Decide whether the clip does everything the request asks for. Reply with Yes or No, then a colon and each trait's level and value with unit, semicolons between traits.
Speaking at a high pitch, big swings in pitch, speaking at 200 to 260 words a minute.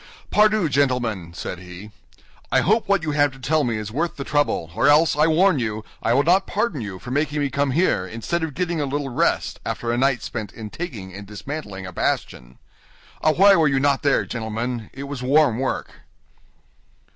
No: low, 135 Hz; wide, 5.9 semitones; fast, 205 wpm